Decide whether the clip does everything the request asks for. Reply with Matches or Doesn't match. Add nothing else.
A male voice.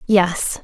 Doesn't match